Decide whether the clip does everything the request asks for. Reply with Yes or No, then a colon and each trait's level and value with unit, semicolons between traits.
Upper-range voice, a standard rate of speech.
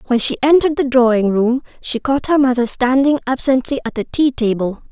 Yes: very high, 255 Hz; average, 195 wpm